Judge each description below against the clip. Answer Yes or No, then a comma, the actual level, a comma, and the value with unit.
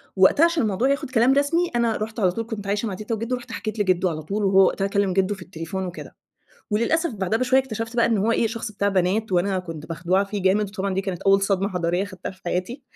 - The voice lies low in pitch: No, high, 200 Hz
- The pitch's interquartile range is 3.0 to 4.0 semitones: Yes, average, 3.4 semitones